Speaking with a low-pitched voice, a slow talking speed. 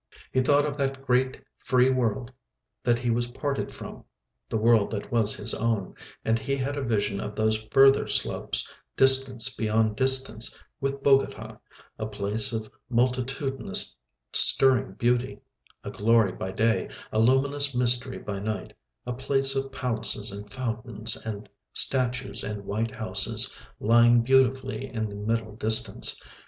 No: low, 120 Hz; average, 145 wpm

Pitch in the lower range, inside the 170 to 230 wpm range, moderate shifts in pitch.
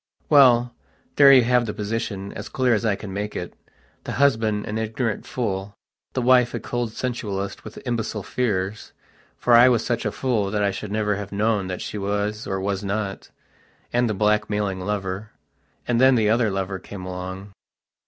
Yes: low, 105 Hz; average, 175 wpm; average, 3.2 semitones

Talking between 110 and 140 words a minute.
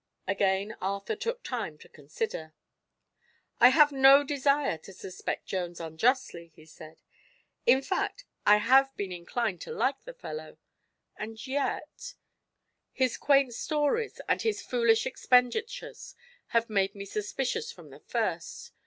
Yes: slow, 135 wpm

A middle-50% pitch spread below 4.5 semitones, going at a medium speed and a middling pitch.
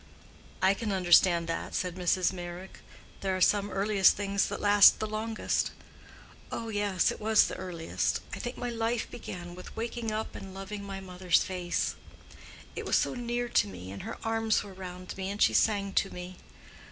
No: average, 2.9 semitones; average, 185 wpm; high, 195 Hz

